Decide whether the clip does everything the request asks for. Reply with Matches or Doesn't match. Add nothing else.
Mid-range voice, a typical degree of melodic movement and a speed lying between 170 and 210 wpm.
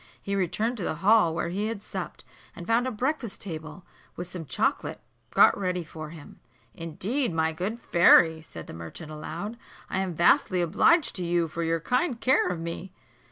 Matches